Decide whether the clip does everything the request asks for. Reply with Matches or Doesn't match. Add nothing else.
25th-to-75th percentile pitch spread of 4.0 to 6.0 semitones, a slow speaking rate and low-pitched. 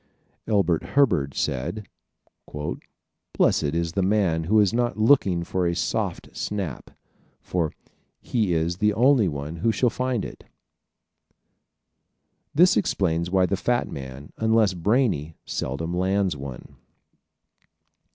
Matches